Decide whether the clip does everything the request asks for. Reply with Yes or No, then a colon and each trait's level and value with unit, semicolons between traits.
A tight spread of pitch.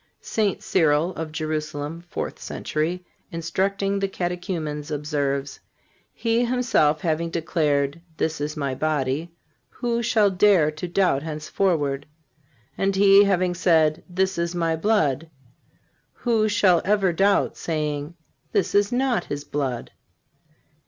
No: average, 4.5 semitones